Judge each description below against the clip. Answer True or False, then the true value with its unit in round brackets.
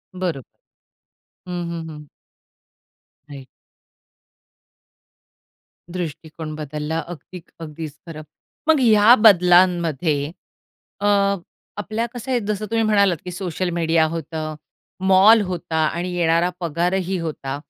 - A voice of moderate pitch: True (170 Hz)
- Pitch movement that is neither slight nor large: True (3.1 semitones)